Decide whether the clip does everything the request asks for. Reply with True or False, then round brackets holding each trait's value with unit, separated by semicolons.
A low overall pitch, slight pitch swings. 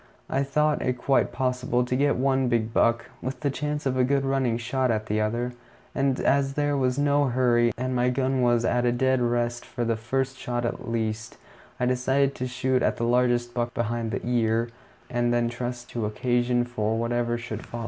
True (125 Hz; 1.8 semitones)